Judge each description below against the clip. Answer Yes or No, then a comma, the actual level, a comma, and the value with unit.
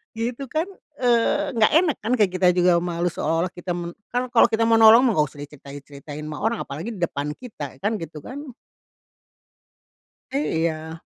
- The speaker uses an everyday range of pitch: No, wide, 6.9 semitones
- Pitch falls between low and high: Yes, medium, 180 Hz